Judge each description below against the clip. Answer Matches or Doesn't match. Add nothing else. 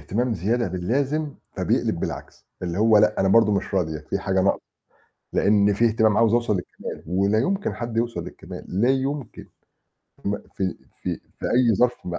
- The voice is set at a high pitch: Doesn't match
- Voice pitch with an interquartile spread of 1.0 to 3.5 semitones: Doesn't match